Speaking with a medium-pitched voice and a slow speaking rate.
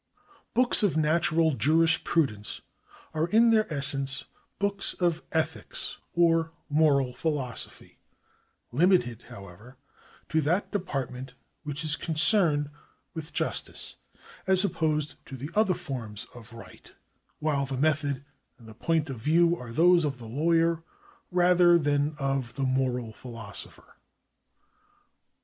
Yes: medium, 150 Hz; slow, 125 wpm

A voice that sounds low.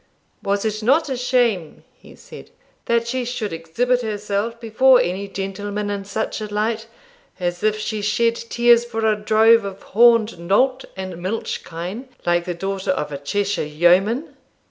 No: high, 210 Hz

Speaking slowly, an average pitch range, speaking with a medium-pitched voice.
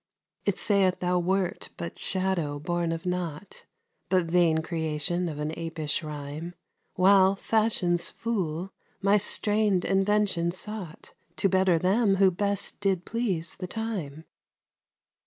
Yes: slow, 125 wpm; average, 3.1 semitones; medium, 180 Hz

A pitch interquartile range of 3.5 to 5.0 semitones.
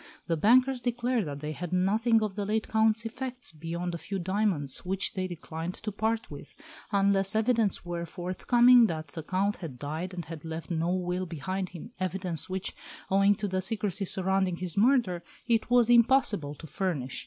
Yes: average, 4.4 semitones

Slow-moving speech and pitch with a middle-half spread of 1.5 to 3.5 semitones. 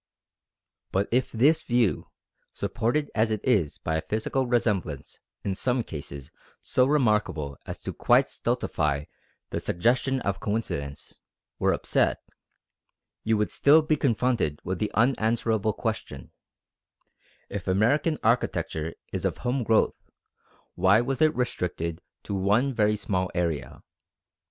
No: slow, 125 wpm; average, 5.3 semitones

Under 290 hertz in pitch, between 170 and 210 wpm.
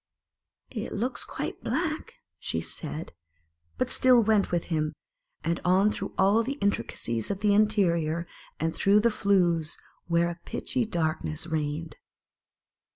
No: medium, 185 Hz; average, 140 wpm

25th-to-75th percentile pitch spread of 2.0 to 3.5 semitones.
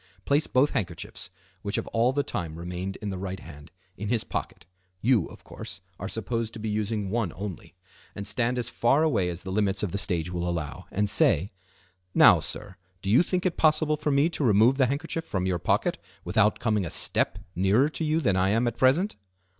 No: average, 5.3 semitones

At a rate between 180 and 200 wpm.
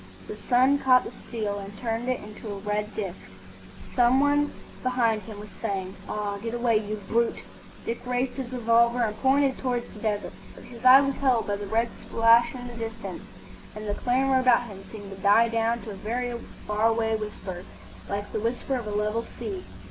Yes: average, 195 wpm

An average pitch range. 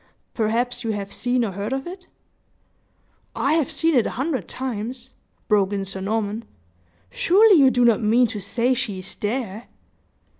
Yes: average, 4.0 semitones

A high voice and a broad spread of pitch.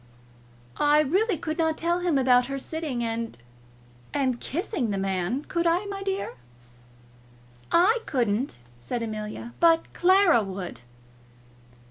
Yes: very high, 285 Hz; wide, 6.8 semitones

